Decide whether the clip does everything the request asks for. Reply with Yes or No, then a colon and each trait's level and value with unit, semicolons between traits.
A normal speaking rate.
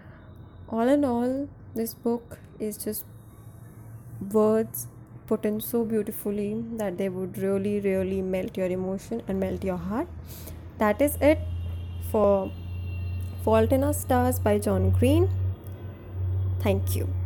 No: slow, 130 wpm